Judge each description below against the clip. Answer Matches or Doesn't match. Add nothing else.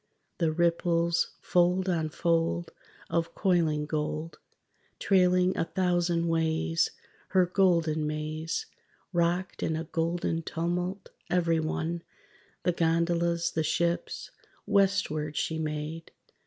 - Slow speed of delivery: Matches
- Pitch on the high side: Doesn't match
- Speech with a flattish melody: Matches